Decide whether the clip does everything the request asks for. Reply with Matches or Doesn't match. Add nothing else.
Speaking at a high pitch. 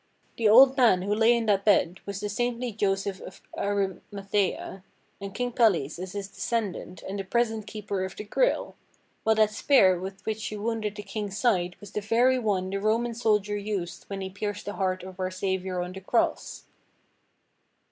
Matches